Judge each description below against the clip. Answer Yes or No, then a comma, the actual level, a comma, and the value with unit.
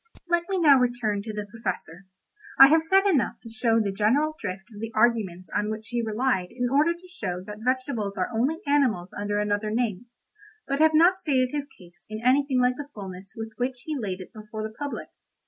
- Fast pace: Yes, fast, 210 wpm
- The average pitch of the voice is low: No, high, 230 Hz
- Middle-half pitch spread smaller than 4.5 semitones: No, average, 5.3 semitones